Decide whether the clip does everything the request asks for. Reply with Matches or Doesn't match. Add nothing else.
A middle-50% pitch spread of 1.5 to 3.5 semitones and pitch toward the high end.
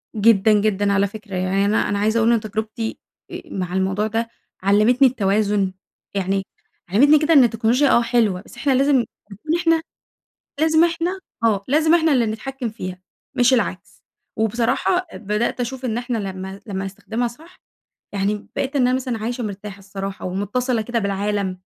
Doesn't match